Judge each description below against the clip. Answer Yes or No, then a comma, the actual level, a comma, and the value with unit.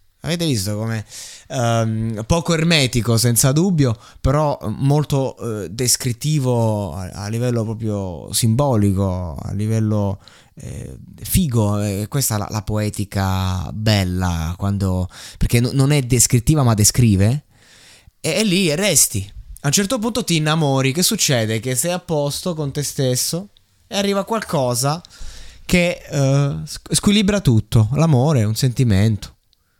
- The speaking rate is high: No, average, 130 wpm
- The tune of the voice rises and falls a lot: Yes, wide, 5.9 semitones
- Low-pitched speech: Yes, low, 120 Hz